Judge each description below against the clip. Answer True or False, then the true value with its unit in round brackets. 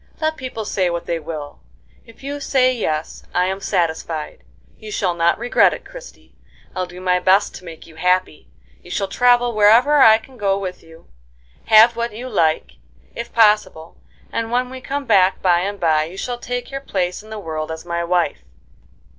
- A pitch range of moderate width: False (5.8 semitones)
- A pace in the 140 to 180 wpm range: False (190 wpm)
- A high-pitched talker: True (195 Hz)